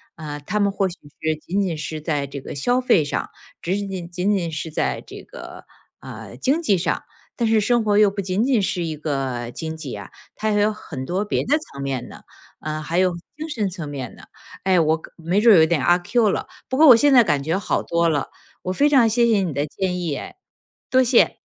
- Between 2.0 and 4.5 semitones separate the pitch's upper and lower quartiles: No, wide, 5.5 semitones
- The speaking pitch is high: No, medium, 180 Hz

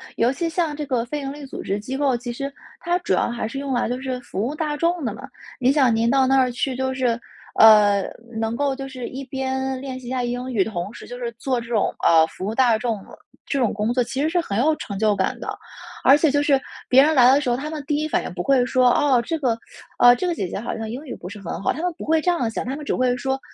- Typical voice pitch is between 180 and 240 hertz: No, very high, 255 Hz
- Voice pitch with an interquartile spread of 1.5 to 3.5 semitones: Yes, average, 3.2 semitones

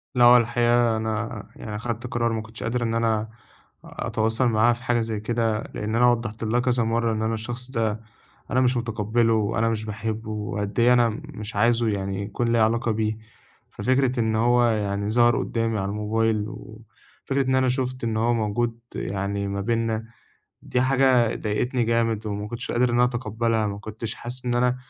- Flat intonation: Yes, narrow, 1.7 semitones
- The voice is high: No, low, 115 Hz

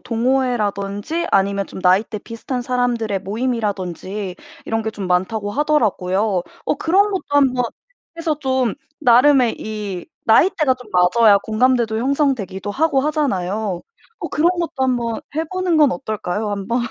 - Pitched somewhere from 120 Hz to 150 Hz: No, high, 230 Hz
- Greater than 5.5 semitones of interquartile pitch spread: No, average, 5.1 semitones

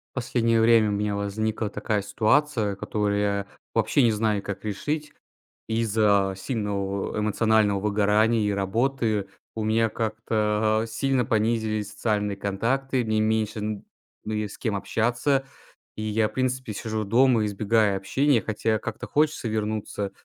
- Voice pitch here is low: Yes, low, 110 Hz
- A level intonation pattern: Yes, narrow, 1.8 semitones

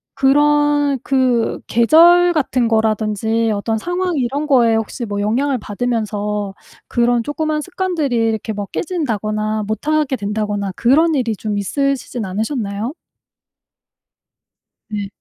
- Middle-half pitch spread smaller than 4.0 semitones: No, wide, 5.4 semitones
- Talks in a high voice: Yes, high, 235 Hz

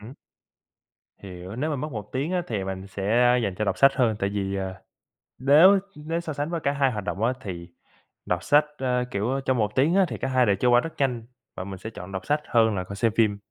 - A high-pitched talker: No, low, 115 Hz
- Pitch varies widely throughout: Yes, wide, 5.9 semitones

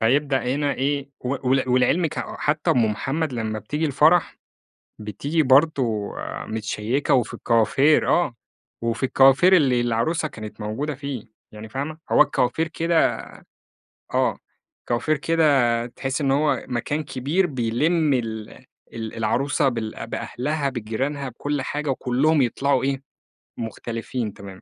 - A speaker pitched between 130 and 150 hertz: Yes, low, 135 Hz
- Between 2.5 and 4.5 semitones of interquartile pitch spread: Yes, average, 4.1 semitones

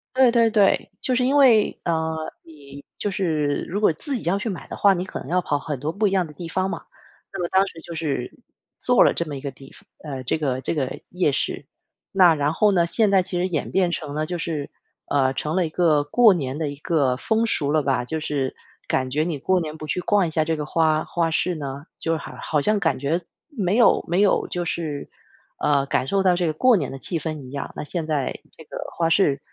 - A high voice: No, medium, 160 Hz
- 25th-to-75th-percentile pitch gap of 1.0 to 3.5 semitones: No, average, 4.4 semitones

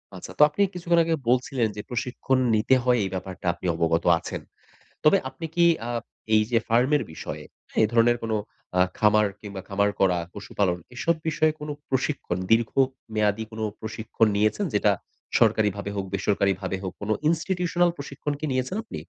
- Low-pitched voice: Yes, low, 115 Hz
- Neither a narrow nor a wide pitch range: No, wide, 5.8 semitones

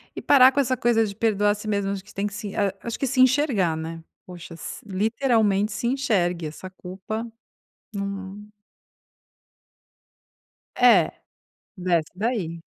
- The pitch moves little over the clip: No, average, 3.9 semitones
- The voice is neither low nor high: No, high, 205 Hz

